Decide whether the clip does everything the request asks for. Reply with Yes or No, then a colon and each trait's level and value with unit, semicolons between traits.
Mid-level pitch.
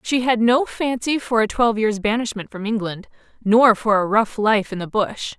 No: high, 220 Hz